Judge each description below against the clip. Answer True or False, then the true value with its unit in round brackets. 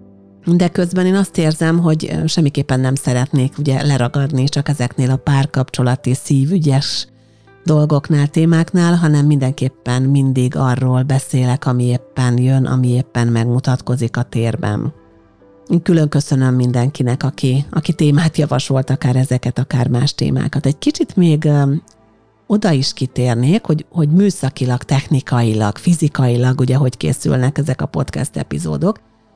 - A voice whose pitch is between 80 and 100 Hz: False (135 Hz)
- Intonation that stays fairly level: False (3.1 semitones)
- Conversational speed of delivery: True (125 wpm)